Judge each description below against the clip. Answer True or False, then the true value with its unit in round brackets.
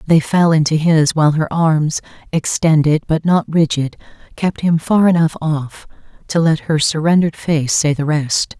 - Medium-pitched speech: True (155 Hz)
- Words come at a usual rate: True (170 wpm)